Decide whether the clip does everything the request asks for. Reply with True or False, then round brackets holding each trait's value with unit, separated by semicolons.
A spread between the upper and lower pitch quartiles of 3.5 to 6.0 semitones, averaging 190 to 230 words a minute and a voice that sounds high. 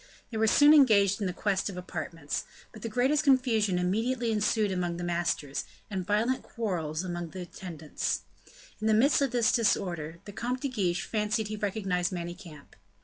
False (4.5 semitones; 170 wpm; 205 Hz)